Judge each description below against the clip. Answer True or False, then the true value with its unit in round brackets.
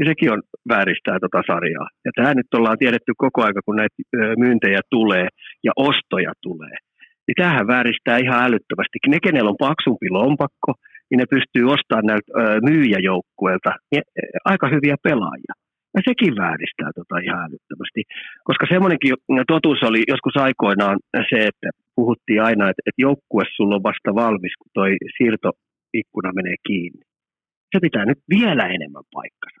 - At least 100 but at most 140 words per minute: False (150 wpm)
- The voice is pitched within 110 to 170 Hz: True (120 Hz)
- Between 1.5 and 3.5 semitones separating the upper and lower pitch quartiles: False (4.3 semitones)